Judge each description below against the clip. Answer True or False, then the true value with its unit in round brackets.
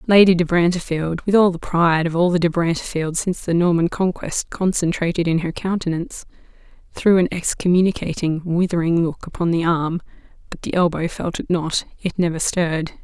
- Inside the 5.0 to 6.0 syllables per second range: True (5.5 syllables/s)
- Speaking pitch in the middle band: True (170 Hz)